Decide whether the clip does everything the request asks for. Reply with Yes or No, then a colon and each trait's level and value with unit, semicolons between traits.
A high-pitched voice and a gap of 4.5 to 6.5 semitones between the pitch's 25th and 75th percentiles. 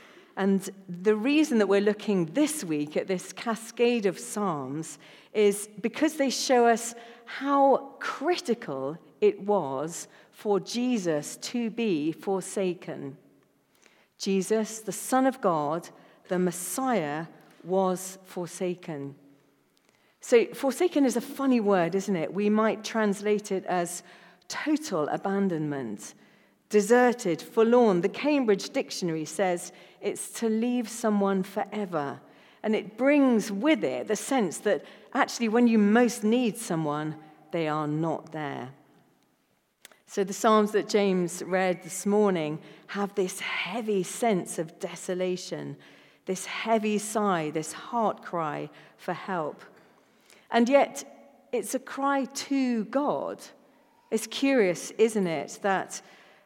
Yes: high, 200 Hz; average, 5.0 semitones